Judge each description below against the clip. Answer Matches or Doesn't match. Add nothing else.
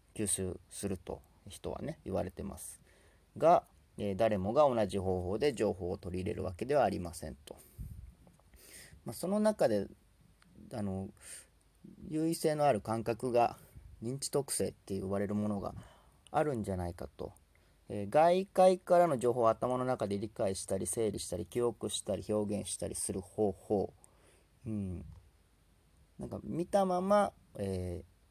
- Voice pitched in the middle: Doesn't match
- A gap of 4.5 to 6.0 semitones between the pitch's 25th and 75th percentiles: Matches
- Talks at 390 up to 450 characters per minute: Doesn't match